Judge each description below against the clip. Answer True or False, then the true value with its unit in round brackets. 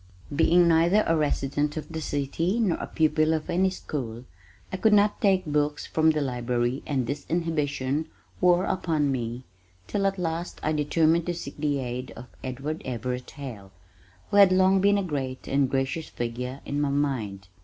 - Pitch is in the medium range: True (150 Hz)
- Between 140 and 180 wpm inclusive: True (175 wpm)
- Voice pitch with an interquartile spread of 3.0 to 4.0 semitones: False (4.5 semitones)